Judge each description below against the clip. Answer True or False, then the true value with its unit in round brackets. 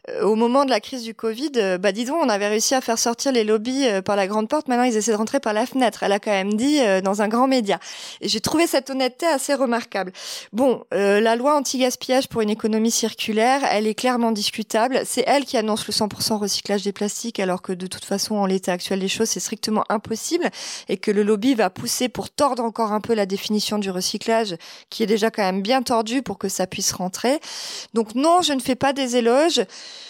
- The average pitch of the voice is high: True (225 Hz)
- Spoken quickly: True (235 wpm)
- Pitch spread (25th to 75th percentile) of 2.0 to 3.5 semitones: False (4.0 semitones)